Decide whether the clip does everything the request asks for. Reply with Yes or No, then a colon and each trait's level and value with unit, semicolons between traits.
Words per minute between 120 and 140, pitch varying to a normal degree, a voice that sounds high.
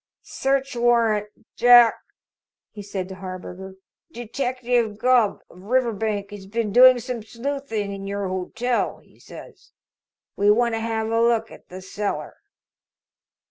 Yes: slow, 135 wpm; average, 3.2 semitones; high, 225 Hz